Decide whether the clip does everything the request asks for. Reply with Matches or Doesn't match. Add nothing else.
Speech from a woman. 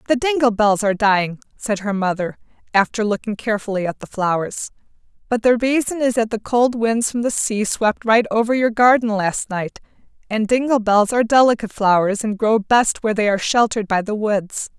Matches